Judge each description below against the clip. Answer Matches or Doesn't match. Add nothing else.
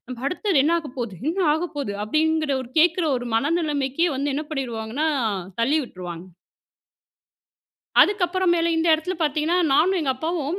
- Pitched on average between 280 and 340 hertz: Matches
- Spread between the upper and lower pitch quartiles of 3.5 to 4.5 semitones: Matches